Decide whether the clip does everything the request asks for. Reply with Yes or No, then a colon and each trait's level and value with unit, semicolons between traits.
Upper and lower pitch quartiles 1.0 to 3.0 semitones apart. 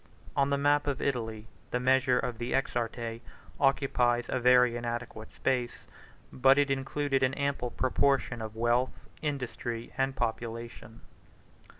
Yes: narrow, 2.5 semitones